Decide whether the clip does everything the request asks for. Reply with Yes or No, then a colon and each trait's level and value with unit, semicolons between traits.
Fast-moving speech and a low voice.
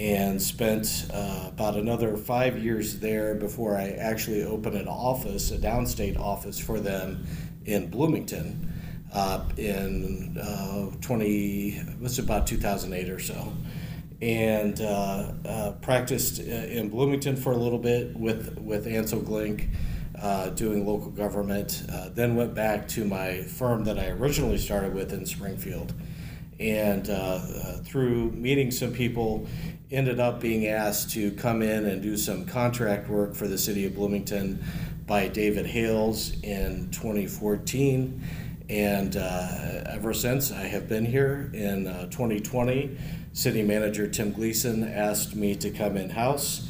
No: average, 145 wpm; low, 105 Hz